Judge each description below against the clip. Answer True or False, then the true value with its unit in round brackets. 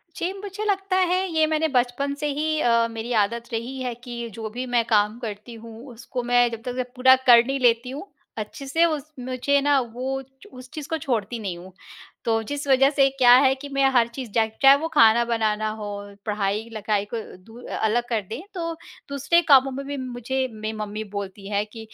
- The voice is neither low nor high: False (245 Hz)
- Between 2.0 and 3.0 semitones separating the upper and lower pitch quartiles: False (3.7 semitones)